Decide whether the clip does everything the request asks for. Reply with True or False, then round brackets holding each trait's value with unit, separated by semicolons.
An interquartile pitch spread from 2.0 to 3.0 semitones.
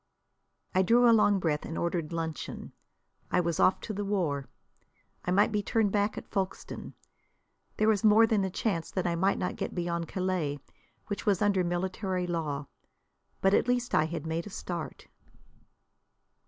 False (3.4 semitones)